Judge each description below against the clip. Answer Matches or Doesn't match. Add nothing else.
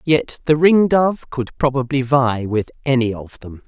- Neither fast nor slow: Matches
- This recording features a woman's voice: Matches